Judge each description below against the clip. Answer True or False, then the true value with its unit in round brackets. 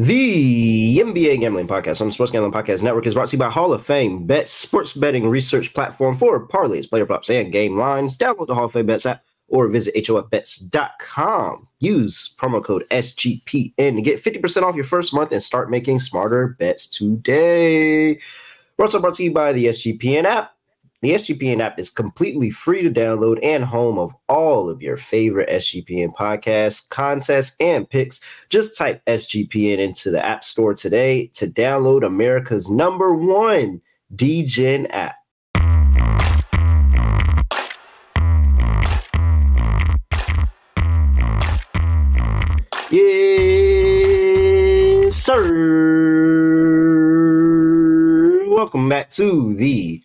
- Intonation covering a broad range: True (7.8 semitones)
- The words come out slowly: True (130 wpm)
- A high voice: False (125 Hz)